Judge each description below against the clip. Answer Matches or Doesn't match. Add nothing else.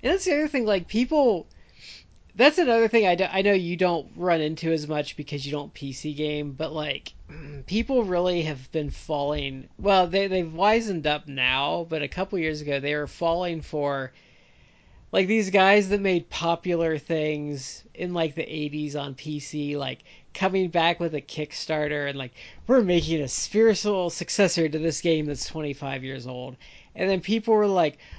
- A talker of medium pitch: Matches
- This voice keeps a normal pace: Matches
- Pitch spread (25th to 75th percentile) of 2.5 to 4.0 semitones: Doesn't match